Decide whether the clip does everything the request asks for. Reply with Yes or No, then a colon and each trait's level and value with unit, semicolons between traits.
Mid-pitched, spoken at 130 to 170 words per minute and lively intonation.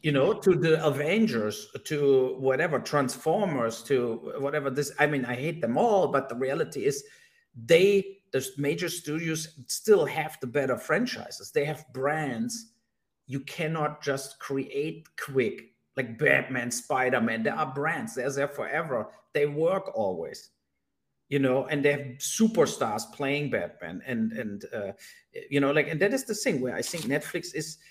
Yes: medium, 150 Hz; average, 160 wpm; wide, 6.2 semitones